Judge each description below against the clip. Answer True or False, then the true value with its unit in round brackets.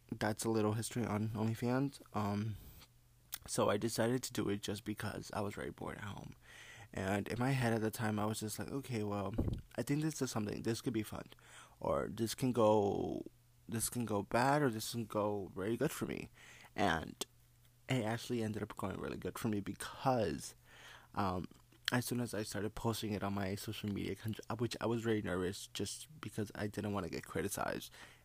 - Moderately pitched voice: False (110 Hz)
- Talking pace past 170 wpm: True (205 wpm)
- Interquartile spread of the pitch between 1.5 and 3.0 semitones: True (2.6 semitones)